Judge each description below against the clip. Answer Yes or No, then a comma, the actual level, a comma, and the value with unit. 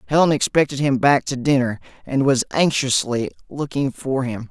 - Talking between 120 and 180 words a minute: Yes, average, 160 wpm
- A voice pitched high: No, low, 135 Hz